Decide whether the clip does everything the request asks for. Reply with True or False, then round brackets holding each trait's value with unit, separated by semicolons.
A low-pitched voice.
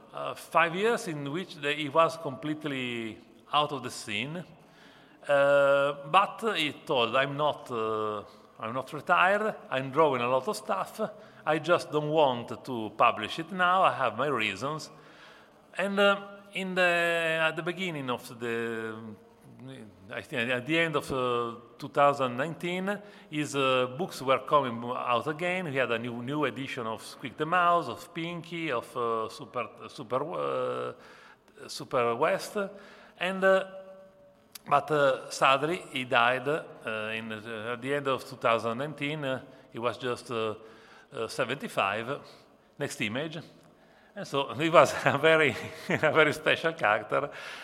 False (145 Hz)